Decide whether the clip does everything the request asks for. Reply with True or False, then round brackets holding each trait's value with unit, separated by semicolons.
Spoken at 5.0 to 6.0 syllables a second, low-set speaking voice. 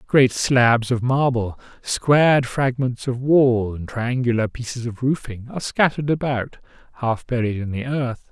False (4.4 syllables/s; 125 Hz)